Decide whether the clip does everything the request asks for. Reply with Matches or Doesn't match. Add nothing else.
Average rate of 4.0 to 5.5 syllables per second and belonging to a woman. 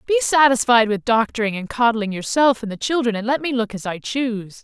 Doesn't match